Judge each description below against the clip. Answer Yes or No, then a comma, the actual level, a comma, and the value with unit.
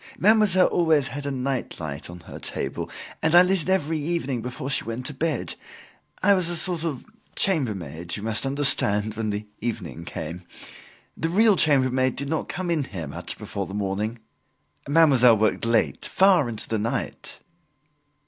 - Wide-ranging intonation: Yes, wide, 7.2 semitones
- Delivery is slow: No, average, 165 wpm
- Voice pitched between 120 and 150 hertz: Yes, low, 135 Hz